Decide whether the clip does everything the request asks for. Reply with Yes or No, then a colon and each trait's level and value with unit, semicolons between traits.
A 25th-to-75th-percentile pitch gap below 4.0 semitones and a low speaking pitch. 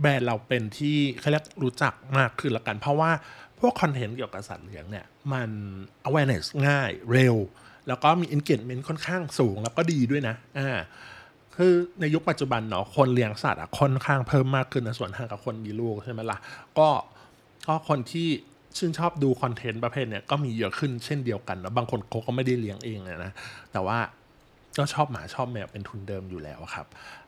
No: average, 4.7 semitones; low, 130 Hz